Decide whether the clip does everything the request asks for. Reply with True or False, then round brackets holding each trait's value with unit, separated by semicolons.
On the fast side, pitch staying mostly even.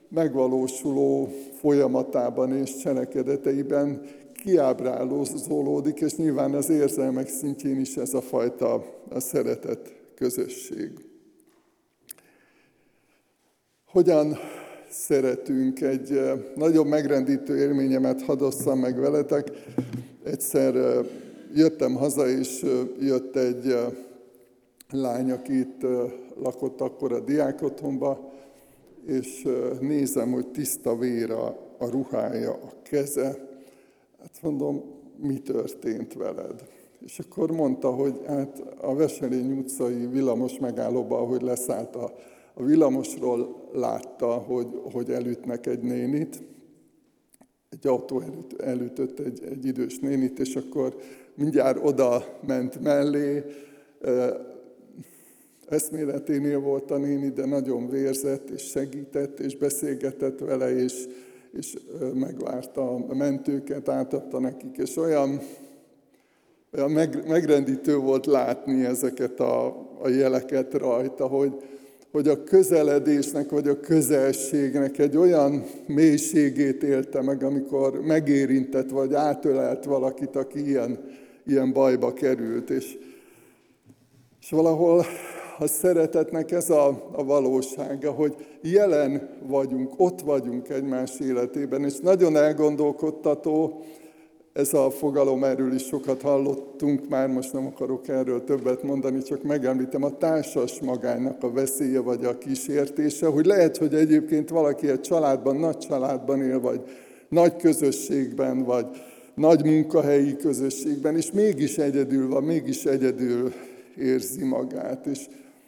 False (110 wpm; 2.2 semitones)